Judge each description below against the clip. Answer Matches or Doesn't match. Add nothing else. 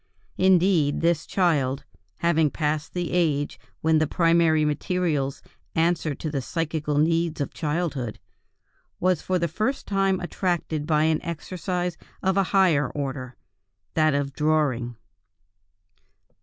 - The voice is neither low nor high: Matches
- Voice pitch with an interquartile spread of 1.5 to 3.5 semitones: Matches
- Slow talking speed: Matches